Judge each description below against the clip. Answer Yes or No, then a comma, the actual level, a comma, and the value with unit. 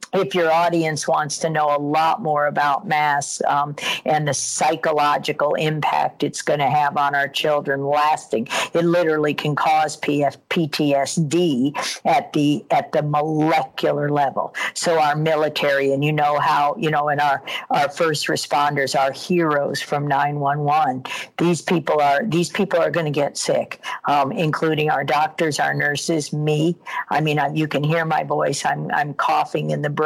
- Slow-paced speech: No, average, 165 wpm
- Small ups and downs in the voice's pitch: Yes, narrow, 2.0 semitones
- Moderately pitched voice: Yes, medium, 150 Hz